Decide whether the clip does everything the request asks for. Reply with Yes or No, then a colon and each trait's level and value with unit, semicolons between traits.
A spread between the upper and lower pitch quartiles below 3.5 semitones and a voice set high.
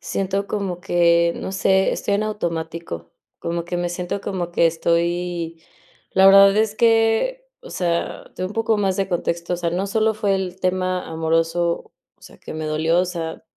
No: average, 2.7 semitones; medium, 180 Hz